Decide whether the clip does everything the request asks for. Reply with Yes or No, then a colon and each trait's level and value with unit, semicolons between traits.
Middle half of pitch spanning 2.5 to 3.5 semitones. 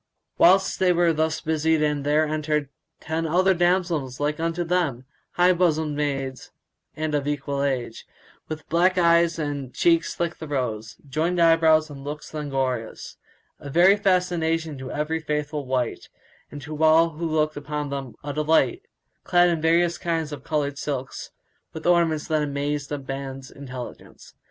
Yes: average, 2.8 semitones